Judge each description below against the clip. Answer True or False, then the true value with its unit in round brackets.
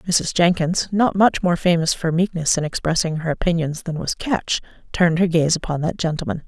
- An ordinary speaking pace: True (195 wpm)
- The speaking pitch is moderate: True (170 Hz)